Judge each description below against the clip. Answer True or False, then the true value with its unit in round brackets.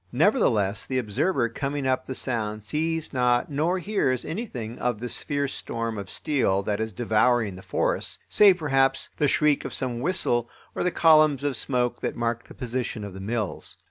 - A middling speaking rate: True (180 wpm)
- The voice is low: True (125 Hz)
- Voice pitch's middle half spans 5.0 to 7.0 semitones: False (4.4 semitones)